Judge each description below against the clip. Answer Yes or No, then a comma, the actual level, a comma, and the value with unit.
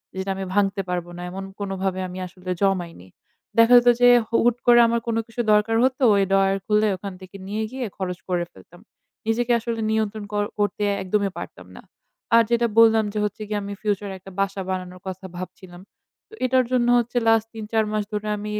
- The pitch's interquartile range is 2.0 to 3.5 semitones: Yes, average, 3.0 semitones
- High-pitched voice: Yes, high, 205 Hz